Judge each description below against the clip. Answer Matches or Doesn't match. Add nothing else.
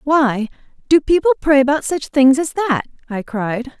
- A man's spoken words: Doesn't match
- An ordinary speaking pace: Matches